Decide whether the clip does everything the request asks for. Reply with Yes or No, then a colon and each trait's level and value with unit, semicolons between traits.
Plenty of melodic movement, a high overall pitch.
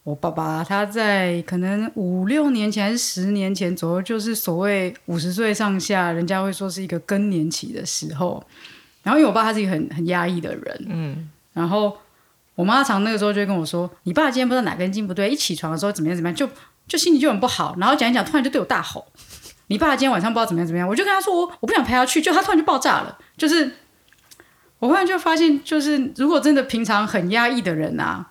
Yes: wide, 7.2 semitones; high, 210 Hz